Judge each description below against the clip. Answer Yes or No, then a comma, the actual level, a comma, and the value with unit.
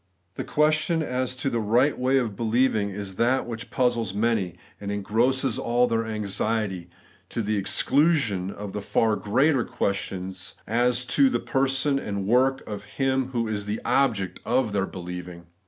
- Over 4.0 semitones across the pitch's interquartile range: Yes, average, 4.4 semitones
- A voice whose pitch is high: No, low, 115 Hz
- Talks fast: No, average, 160 wpm